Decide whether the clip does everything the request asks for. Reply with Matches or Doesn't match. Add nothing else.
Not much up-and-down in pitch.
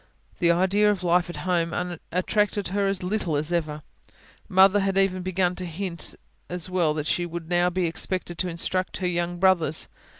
Matches